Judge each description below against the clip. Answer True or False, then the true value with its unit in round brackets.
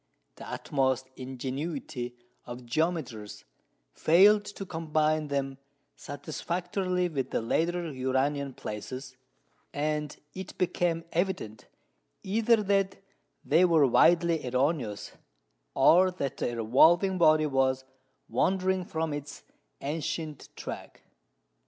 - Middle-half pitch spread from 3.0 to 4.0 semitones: False (4.9 semitones)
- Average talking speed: False (100 wpm)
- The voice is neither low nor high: True (155 Hz)